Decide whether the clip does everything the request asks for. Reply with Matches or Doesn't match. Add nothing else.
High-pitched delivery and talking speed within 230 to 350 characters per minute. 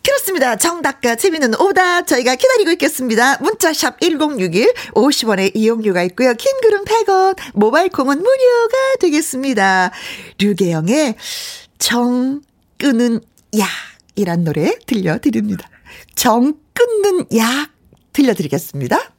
Matches